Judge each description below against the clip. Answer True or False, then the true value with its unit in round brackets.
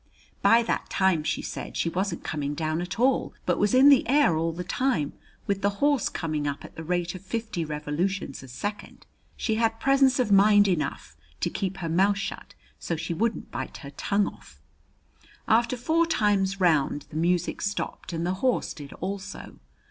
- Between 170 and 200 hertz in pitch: True (190 Hz)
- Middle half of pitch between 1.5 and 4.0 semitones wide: False (5.1 semitones)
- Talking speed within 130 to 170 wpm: False (185 wpm)